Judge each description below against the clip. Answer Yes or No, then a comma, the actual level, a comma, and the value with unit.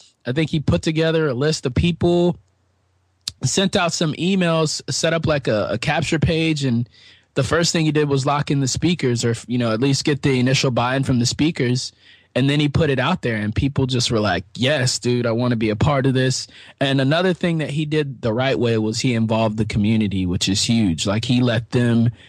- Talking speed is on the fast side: Yes, fast, 235 wpm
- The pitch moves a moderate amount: Yes, average, 4.9 semitones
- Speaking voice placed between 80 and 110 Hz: No, low, 130 Hz